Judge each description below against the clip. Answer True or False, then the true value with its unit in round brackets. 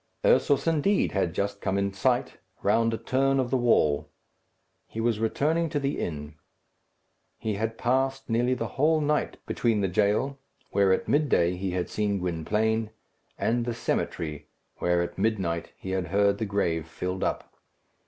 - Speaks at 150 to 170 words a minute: True (165 wpm)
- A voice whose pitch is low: True (105 Hz)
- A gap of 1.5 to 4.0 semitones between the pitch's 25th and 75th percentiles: False (5.3 semitones)